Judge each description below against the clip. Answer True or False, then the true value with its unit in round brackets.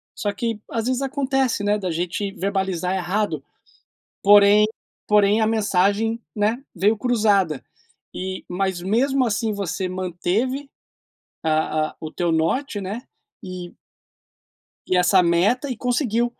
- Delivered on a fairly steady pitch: False (3.8 semitones)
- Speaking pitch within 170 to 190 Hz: False (205 Hz)